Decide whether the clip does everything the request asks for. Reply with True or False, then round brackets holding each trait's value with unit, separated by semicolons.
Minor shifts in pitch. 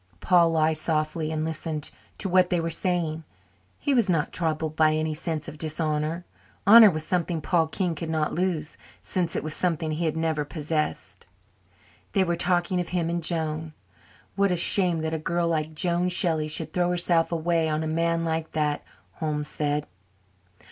True (2.0 semitones)